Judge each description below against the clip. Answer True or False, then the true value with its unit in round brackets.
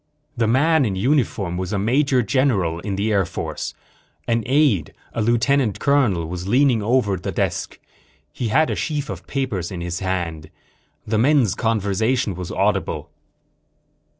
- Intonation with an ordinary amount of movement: False (5.9 semitones)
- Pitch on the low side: True (110 Hz)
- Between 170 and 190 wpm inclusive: False (150 wpm)